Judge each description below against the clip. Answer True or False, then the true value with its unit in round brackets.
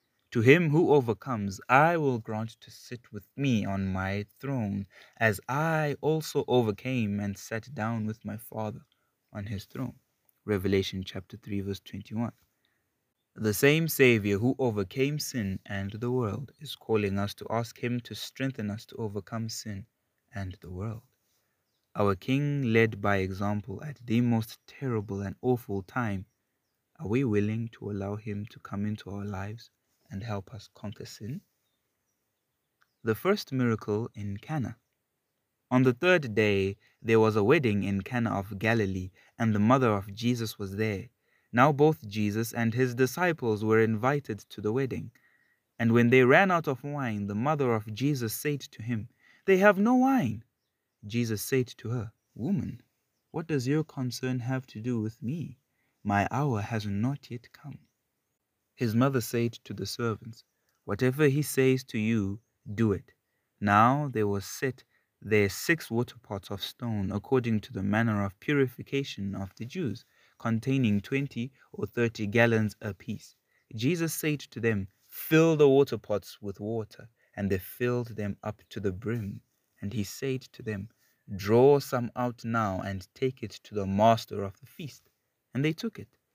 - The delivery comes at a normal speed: True (165 wpm)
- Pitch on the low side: True (115 Hz)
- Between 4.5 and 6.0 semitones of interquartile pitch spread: False (3.9 semitones)